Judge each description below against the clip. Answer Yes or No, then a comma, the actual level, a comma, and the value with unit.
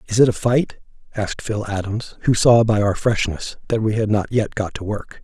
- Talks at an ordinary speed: No, fast, 230 wpm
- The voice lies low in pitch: Yes, low, 110 Hz